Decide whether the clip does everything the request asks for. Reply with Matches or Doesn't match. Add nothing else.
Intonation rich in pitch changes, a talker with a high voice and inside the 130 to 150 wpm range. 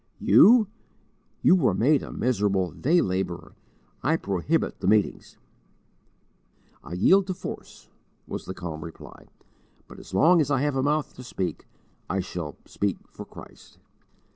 Doesn't match